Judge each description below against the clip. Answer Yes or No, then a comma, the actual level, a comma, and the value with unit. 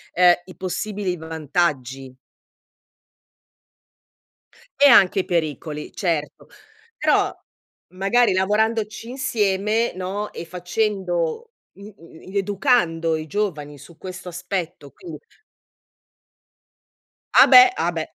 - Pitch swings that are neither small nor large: Yes, average, 4.3 semitones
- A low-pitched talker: No, medium, 185 Hz